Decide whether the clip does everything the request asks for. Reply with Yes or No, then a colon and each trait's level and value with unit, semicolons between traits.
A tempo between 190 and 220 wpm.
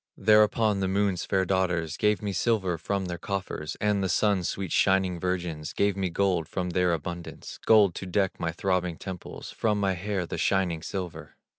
No: average, 180 wpm